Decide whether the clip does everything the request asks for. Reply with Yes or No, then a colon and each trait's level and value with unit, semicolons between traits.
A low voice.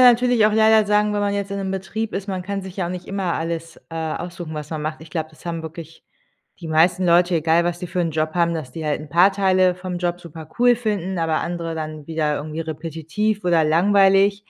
No: medium, 175 Hz